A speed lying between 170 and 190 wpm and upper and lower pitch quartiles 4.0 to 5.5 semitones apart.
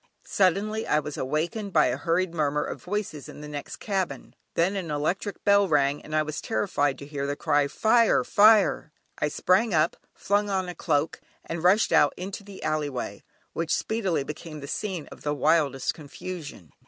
Yes: average, 185 wpm; average, 5.0 semitones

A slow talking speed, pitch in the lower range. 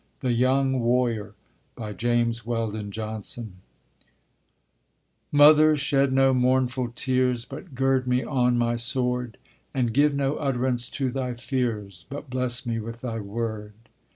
Yes: slow, 125 wpm; low, 125 Hz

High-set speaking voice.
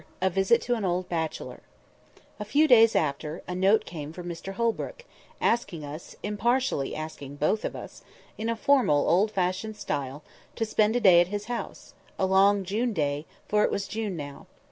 Yes: high, 195 Hz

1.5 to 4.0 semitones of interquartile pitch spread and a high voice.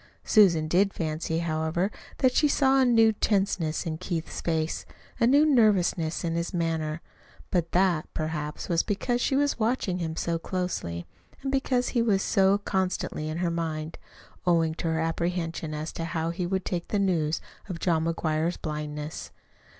No: average, 3.7 semitones; medium, 170 Hz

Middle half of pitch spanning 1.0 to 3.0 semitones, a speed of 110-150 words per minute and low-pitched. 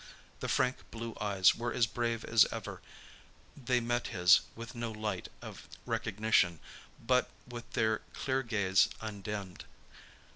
Yes: narrow, 2.6 semitones; slow, 135 wpm; low, 115 Hz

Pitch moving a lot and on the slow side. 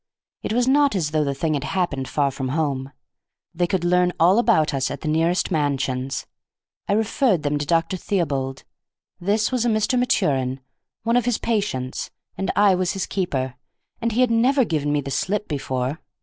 No: wide, 7.0 semitones; average, 190 wpm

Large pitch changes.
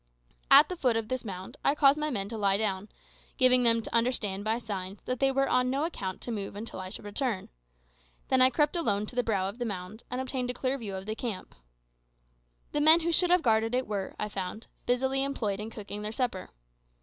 No: average, 4.3 semitones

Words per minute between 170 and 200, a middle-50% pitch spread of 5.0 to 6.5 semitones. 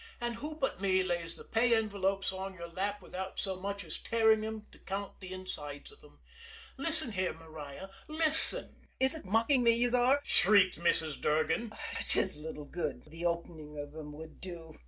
Yes: average, 185 wpm; average, 5.3 semitones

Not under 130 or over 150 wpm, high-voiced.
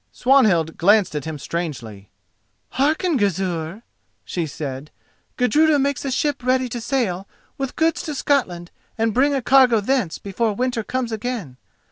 Yes: average, 145 wpm; high, 225 Hz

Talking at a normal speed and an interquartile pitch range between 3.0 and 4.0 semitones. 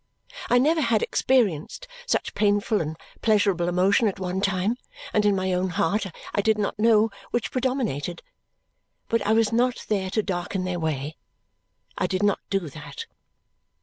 Yes: average, 160 wpm; average, 3.6 semitones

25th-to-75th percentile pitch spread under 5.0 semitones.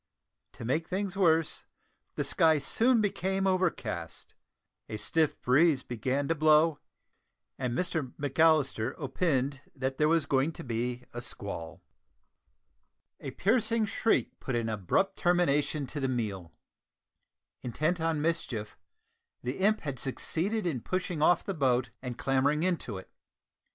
No: wide, 5.6 semitones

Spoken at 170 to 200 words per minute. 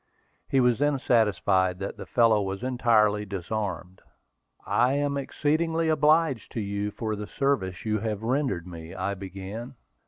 No: average, 150 wpm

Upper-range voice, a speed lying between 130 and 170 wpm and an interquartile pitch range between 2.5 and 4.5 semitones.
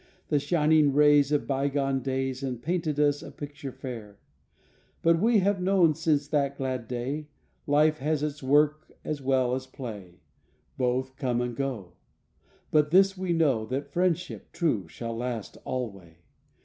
No: medium, 140 Hz; average, 150 wpm; average, 3.3 semitones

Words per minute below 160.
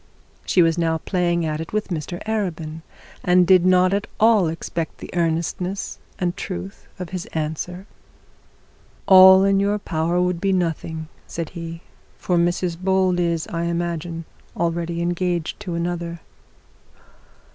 Yes: average, 140 wpm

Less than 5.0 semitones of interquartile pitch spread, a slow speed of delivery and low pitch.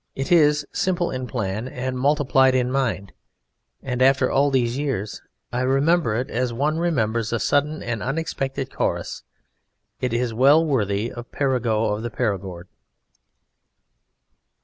No: average, 3.4 semitones; average, 145 wpm; low, 130 Hz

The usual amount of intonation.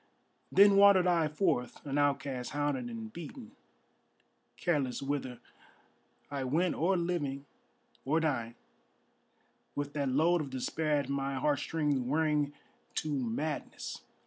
Yes: average, 3.2 semitones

